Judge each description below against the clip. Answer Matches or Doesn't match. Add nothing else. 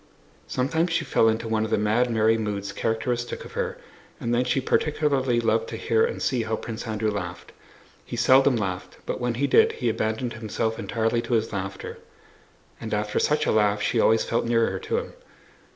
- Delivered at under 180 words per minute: Doesn't match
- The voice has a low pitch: Matches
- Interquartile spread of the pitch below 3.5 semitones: Matches